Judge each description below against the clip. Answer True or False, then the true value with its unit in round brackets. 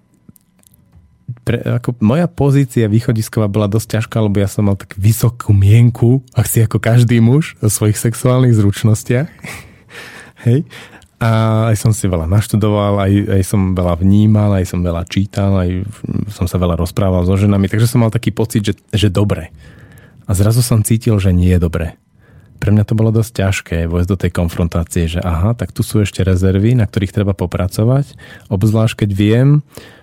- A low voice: True (105 Hz)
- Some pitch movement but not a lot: True (3.1 semitones)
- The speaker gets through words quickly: True (175 wpm)